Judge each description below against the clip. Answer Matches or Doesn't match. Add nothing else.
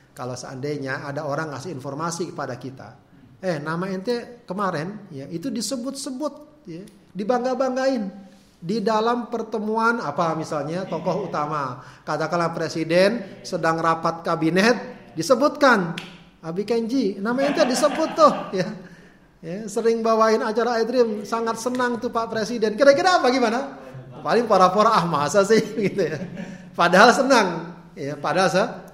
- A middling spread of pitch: Doesn't match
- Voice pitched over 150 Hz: Matches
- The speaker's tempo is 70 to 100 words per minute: Doesn't match